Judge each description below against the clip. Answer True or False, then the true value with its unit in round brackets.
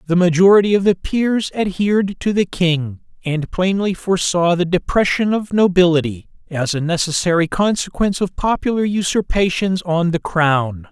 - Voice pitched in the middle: True (180 Hz)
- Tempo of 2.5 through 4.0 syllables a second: False (4.9 syllables/s)